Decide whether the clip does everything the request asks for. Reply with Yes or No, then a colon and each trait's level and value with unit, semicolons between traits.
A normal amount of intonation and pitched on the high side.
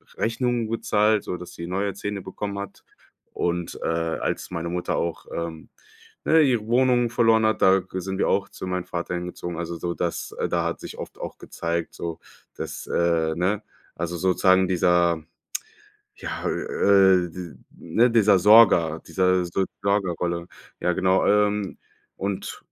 No: average, 3.1 semitones; very low, 95 Hz